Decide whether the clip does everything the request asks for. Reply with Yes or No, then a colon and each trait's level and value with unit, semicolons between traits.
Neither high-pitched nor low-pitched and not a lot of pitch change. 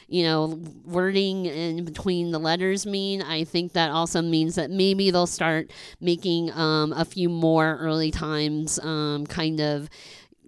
Yes: medium, 165 Hz; narrow, 2.2 semitones